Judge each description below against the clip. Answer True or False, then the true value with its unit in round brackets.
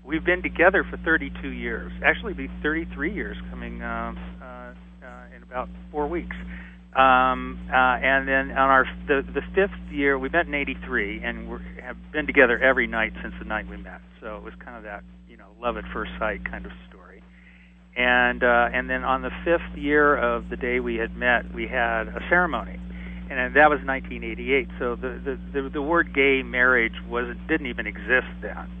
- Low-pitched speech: True (90 Hz)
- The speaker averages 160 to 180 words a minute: False (200 wpm)